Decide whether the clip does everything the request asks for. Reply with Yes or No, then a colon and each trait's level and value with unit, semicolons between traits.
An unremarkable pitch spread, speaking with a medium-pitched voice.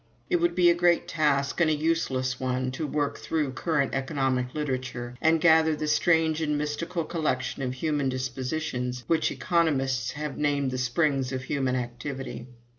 Yes: average, 3.6 semitones; medium, 145 Hz